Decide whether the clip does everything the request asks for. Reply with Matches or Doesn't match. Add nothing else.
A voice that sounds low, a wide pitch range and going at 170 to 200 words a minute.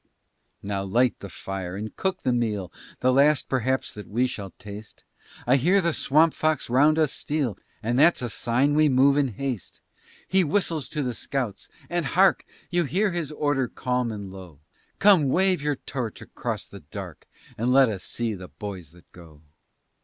Matches